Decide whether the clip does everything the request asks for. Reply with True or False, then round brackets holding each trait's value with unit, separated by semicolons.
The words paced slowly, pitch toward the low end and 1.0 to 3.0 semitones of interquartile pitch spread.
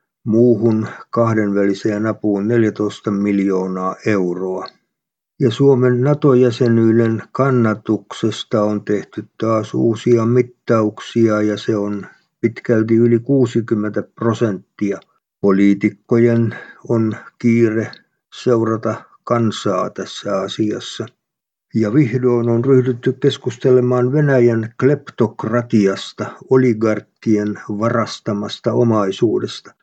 True (80 wpm; 115 Hz; 2.4 semitones)